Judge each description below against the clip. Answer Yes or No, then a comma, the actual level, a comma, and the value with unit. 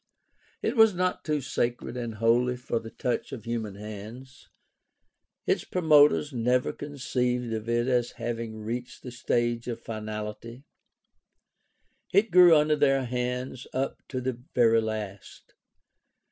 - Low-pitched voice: Yes, low, 120 Hz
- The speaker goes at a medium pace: No, slow, 130 wpm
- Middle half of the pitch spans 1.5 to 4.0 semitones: Yes, narrow, 2.5 semitones